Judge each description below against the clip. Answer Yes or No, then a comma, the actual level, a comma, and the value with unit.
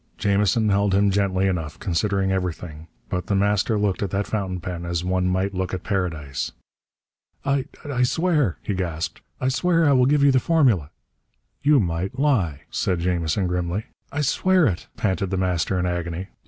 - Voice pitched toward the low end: Yes, very low, 95 Hz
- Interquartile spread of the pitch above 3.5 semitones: Yes, average, 4.4 semitones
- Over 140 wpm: Yes, average, 175 wpm